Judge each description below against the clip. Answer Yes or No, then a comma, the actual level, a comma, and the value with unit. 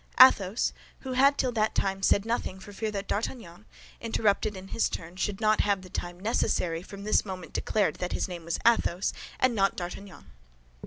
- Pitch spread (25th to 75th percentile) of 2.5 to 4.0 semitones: Yes, average, 3.1 semitones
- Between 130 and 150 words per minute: No, average, 190 wpm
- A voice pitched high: Yes, high, 200 Hz